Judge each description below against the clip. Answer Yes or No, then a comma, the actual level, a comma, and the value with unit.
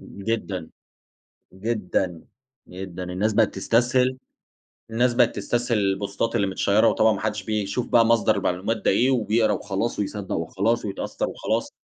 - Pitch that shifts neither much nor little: Yes, average, 3.1 semitones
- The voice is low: Yes, low, 105 Hz